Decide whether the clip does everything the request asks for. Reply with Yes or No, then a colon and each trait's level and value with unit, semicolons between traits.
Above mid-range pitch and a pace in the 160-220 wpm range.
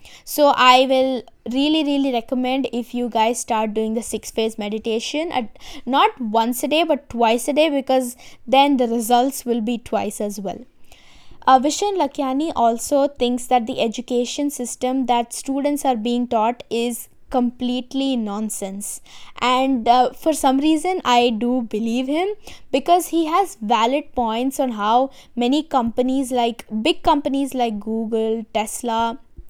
No: very high, 250 Hz; average, 150 wpm